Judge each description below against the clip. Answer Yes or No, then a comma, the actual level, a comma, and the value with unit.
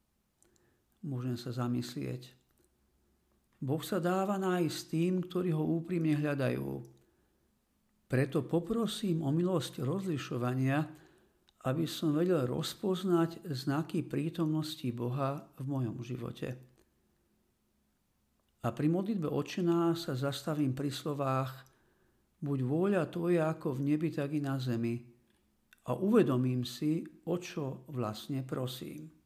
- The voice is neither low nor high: Yes, medium, 150 Hz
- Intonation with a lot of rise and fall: No, average, 4.7 semitones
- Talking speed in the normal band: No, slow, 105 wpm